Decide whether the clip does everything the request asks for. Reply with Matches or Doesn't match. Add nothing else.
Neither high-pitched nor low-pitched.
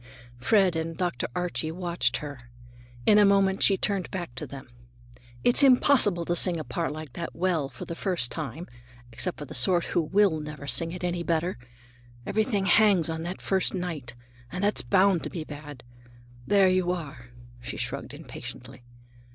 Matches